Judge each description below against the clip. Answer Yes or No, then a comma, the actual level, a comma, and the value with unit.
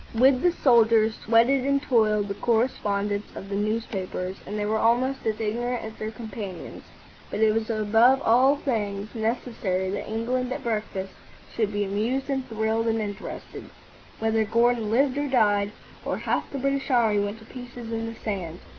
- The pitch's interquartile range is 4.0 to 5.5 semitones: No, average, 2.8 semitones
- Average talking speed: Yes, average, 170 wpm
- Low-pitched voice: No, high, 225 Hz